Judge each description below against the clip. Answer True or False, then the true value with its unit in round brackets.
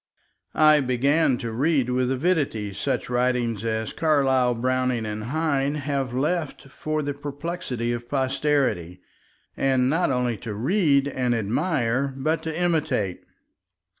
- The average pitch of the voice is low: True (130 Hz)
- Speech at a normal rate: False (130 wpm)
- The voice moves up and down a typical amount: True (3.8 semitones)